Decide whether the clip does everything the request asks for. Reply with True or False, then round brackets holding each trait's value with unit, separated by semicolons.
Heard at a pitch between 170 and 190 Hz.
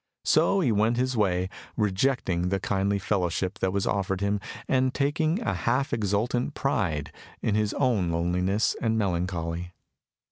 False (100 Hz)